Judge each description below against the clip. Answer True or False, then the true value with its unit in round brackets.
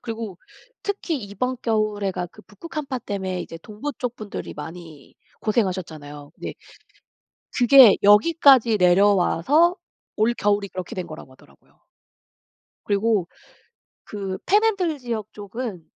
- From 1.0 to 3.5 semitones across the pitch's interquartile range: False (5.2 semitones)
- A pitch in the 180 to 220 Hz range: True (210 Hz)